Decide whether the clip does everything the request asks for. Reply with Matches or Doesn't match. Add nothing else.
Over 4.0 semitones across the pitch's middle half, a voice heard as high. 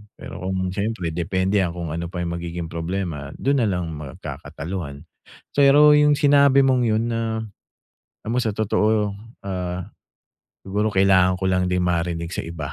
Doesn't match